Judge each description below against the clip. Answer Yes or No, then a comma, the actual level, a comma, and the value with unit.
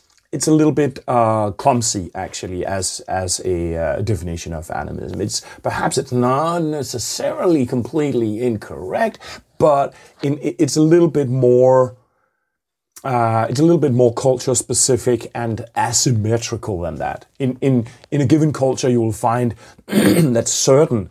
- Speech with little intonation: No, average, 3.7 semitones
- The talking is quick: No, average, 145 wpm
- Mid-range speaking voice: No, low, 125 Hz